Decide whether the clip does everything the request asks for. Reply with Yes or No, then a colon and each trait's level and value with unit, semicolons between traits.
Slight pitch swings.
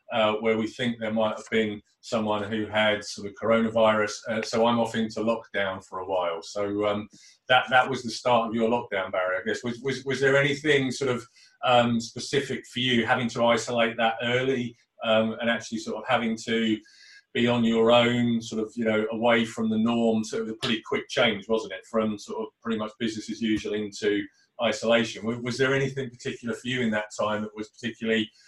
Yes: narrow, 1.8 semitones